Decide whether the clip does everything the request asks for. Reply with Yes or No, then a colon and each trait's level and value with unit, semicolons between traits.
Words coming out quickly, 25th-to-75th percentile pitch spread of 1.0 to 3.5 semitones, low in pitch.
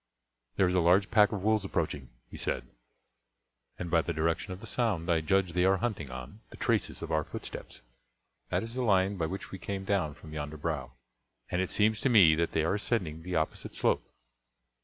No: fast, 210 wpm; average, 4.1 semitones; very low, 90 Hz